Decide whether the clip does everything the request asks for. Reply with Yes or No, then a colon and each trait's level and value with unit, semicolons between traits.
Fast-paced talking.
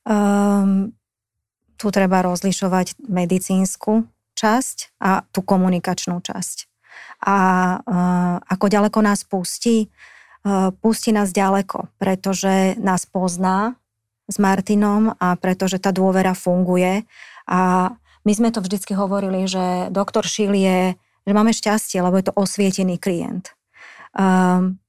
No: average, 120 wpm